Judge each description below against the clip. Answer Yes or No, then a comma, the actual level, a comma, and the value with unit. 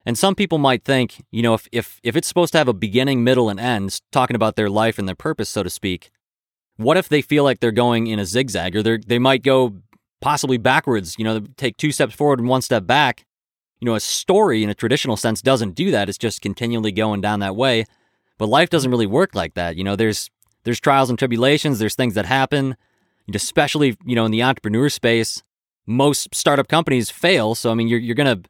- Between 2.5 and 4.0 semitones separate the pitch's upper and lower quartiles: Yes, average, 3.7 semitones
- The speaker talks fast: Yes, fast, 230 wpm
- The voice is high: No, low, 120 Hz